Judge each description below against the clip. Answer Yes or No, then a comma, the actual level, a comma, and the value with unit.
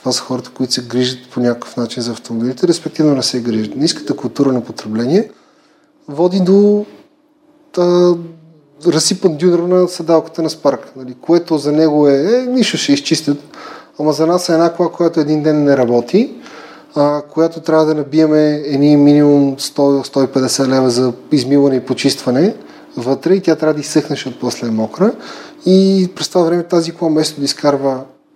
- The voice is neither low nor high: Yes, medium, 150 Hz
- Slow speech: No, fast, 165 wpm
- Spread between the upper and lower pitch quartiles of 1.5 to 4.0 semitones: No, average, 4.4 semitones